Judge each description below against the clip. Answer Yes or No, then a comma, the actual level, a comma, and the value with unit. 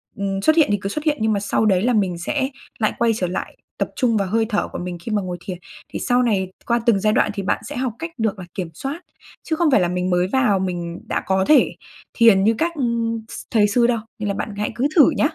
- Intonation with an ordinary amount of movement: Yes, average, 4.3 semitones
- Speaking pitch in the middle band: No, high, 210 Hz